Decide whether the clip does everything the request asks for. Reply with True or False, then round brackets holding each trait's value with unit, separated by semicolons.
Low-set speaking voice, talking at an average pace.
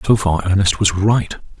True (100 Hz; 190 wpm)